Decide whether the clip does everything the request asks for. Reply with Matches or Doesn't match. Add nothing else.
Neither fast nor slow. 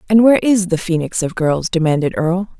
Doesn't match